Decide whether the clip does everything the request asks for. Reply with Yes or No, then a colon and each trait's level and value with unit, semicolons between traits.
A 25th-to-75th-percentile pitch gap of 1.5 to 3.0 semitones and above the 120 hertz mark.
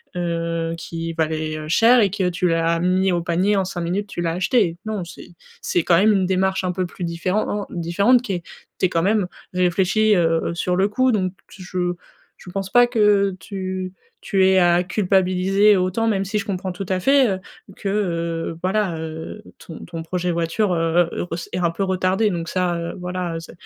Yes: average, 2.7 semitones; medium, 185 Hz